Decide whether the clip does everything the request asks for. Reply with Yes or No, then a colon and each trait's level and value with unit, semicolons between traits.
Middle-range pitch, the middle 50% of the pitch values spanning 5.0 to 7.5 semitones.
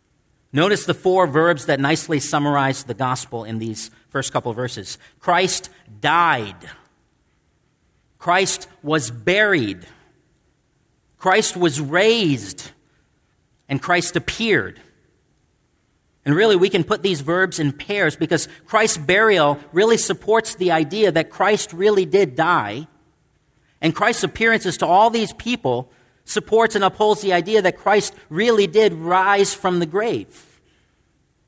Yes: medium, 175 Hz; wide, 5.4 semitones